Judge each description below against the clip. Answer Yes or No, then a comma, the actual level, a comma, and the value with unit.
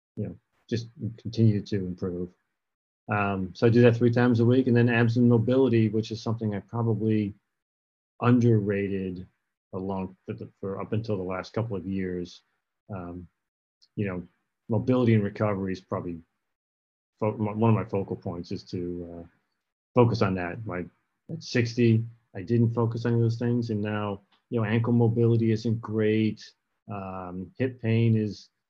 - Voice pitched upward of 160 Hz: No, low, 110 Hz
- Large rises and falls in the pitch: No, average, 3.6 semitones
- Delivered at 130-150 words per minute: No, average, 160 wpm